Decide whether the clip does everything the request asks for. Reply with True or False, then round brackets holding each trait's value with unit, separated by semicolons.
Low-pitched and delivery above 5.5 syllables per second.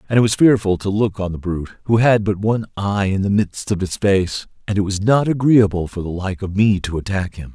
True (100 Hz; 5.7 syllables/s)